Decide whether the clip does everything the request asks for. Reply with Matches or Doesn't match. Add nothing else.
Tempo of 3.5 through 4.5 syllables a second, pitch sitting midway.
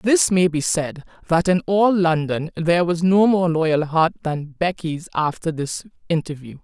Matches